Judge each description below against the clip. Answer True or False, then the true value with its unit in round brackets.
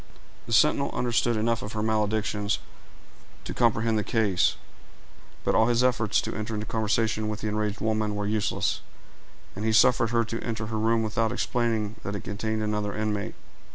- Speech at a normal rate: True (175 wpm)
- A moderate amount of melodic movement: False (1.2 semitones)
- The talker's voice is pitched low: True (110 Hz)